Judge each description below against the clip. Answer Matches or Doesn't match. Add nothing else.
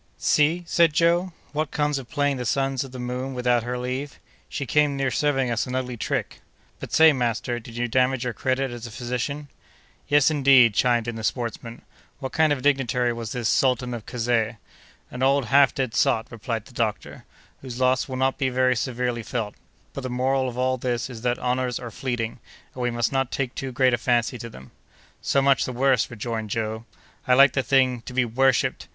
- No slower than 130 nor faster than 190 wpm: Doesn't match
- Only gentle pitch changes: Matches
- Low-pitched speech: Matches